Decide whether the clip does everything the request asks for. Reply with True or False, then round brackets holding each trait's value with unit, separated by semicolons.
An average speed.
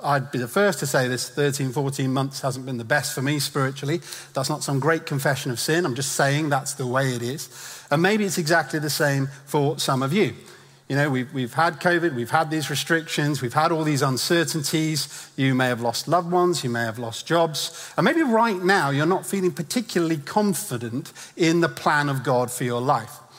False (215 wpm)